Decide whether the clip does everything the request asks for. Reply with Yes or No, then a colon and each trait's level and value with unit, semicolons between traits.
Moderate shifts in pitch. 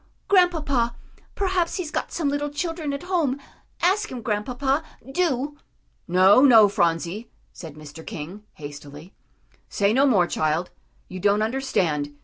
No: wide, 8.9 semitones